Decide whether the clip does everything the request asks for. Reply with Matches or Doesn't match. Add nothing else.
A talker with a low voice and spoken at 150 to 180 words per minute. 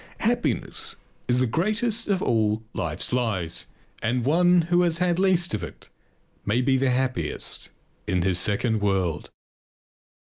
Doesn't match